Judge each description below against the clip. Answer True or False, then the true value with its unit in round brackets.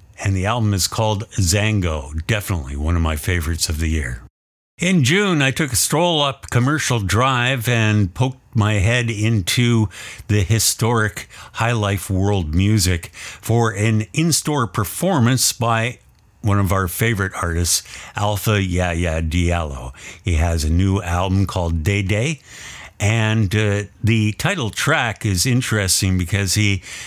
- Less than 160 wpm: True (145 wpm)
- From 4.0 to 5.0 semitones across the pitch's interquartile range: True (4.3 semitones)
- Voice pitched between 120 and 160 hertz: False (105 Hz)